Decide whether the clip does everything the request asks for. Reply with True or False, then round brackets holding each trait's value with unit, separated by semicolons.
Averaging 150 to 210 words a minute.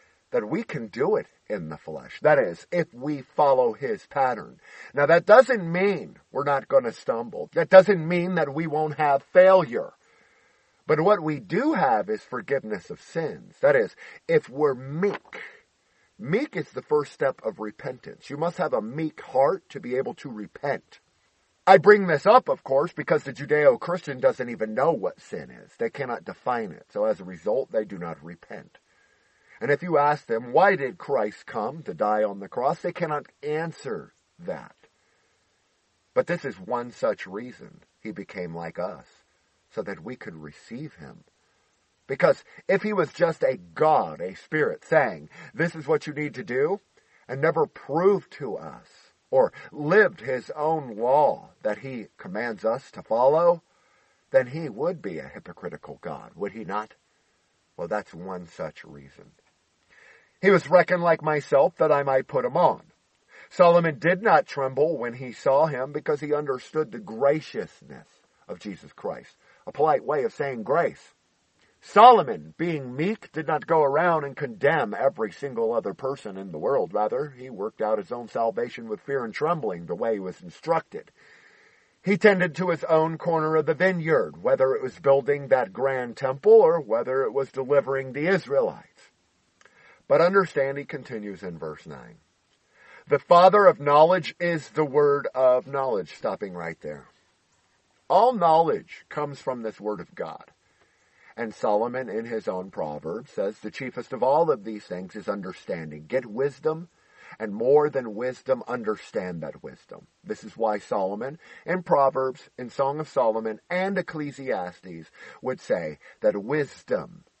True (170 wpm)